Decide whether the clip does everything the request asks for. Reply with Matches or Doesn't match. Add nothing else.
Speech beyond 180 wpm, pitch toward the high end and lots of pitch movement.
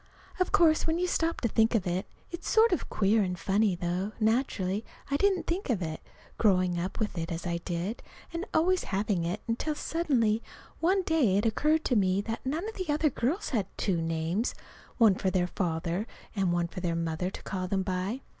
Matches